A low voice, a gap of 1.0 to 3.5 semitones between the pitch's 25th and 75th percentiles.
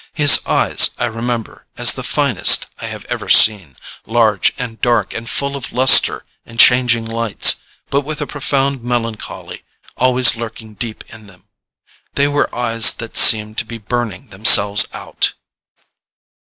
Yes: low, 115 Hz; narrow, 2.4 semitones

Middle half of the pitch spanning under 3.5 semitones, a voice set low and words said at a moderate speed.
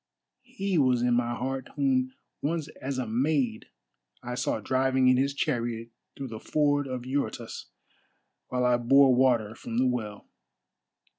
Yes: narrow, 2.4 semitones; low, 130 Hz; average, 150 wpm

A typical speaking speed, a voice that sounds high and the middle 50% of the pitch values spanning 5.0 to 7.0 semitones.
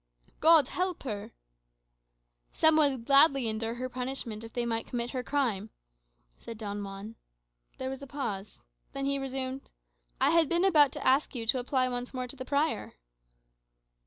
No: average, 165 wpm; very high, 255 Hz; average, 3.5 semitones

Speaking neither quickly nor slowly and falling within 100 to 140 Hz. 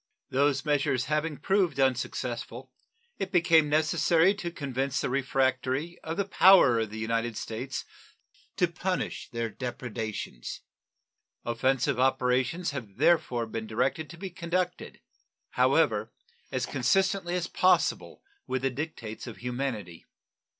No: slow, 120 wpm; low, 135 Hz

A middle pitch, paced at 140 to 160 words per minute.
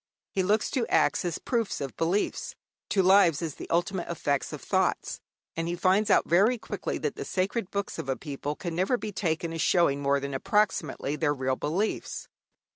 No: medium, 175 Hz; average, 195 wpm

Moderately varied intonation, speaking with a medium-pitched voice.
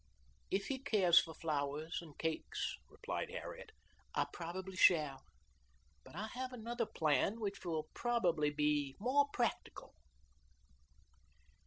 No: wide, 6.9 semitones; medium, 175 Hz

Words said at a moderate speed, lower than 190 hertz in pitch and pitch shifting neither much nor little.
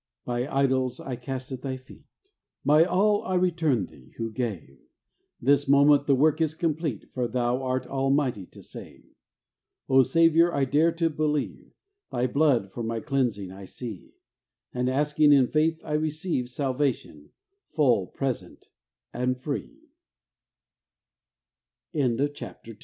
No: slow, 120 wpm; low, 135 Hz; average, 3.7 semitones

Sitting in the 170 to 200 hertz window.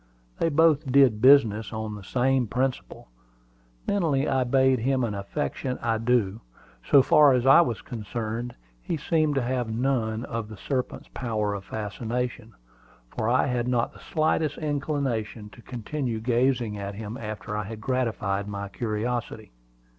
No: low, 120 Hz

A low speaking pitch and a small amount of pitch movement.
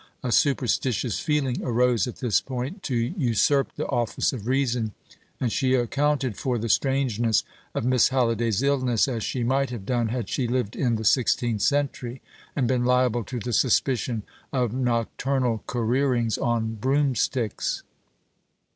Yes: low, 125 Hz; narrow, 2.3 semitones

